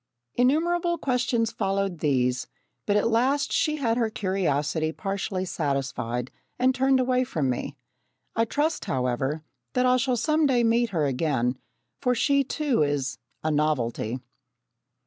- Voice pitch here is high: Yes, high, 205 Hz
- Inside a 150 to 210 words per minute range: No, average, 140 wpm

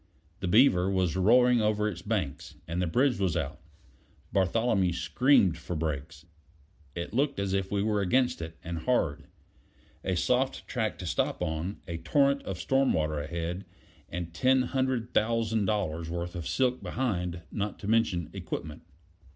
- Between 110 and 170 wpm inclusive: Yes, average, 160 wpm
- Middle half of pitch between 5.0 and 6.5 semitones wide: Yes, wide, 5.4 semitones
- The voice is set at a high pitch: No, very low, 95 Hz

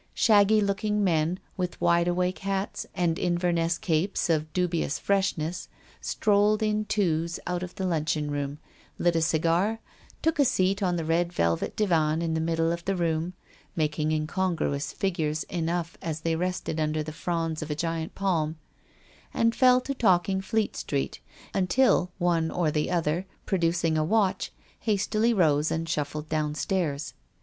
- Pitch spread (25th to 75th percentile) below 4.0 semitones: Yes, average, 3.3 semitones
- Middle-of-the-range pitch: Yes, medium, 170 Hz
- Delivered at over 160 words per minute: No, average, 155 wpm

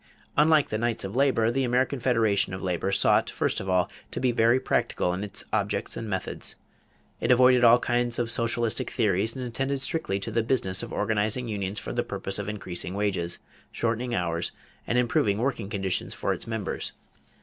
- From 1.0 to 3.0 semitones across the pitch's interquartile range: No, average, 3.8 semitones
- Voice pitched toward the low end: Yes, low, 115 Hz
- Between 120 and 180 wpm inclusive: No, average, 190 wpm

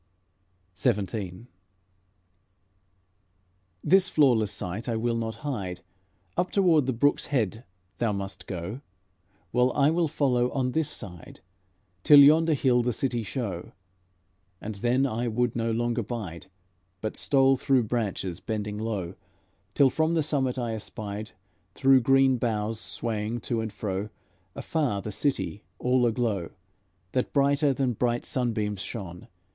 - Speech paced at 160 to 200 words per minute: No, slow, 135 wpm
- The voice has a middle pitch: No, low, 120 Hz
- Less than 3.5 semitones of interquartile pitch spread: No, average, 4.1 semitones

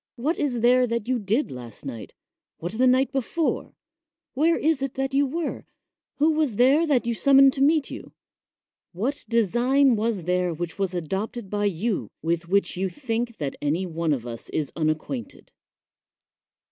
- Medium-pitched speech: No, high, 235 Hz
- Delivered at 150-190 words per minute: Yes, average, 180 wpm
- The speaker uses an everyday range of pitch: No, wide, 7.3 semitones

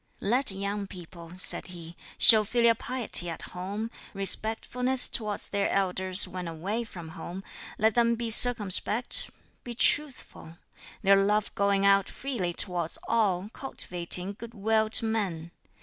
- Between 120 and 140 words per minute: Yes, slow, 135 wpm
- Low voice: No, high, 200 Hz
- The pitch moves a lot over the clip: No, average, 3.8 semitones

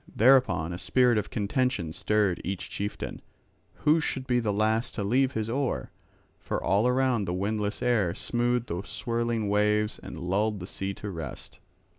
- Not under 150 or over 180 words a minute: Yes, average, 165 wpm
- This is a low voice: Yes, low, 110 Hz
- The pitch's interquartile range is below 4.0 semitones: Yes, average, 3.6 semitones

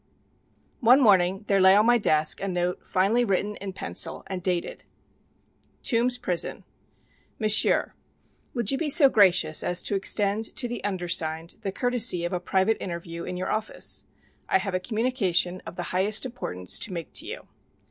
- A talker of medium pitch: No, high, 195 Hz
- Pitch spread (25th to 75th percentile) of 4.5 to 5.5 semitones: No, average, 3.9 semitones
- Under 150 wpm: No, average, 170 wpm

